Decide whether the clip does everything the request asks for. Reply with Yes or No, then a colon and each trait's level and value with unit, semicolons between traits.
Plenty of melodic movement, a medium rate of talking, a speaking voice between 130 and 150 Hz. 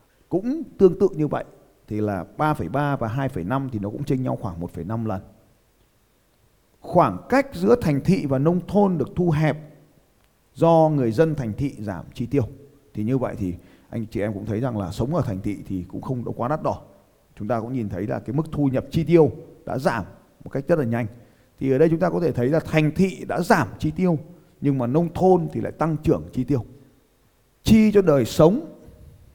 Yes: wide, 6.2 semitones; average, 220 wpm; low, 135 Hz